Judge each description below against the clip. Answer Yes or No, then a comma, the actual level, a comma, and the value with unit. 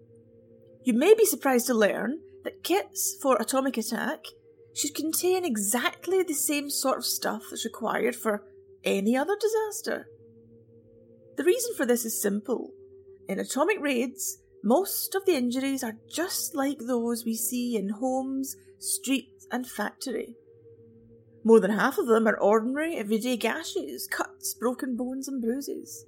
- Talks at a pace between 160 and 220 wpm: No, average, 145 wpm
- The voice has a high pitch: Yes, very high, 265 Hz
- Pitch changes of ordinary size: No, wide, 8.8 semitones